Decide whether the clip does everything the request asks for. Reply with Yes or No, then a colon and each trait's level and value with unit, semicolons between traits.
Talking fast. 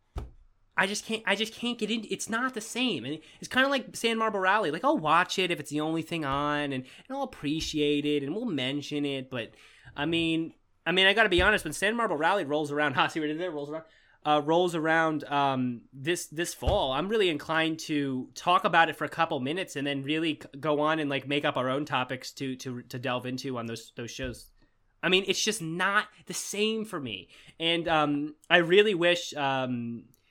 Yes: fast, 225 wpm